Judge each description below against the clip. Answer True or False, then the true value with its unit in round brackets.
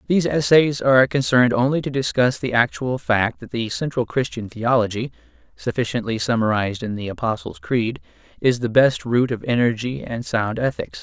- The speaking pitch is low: True (120 Hz)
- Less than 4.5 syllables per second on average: True (4.2 syllables/s)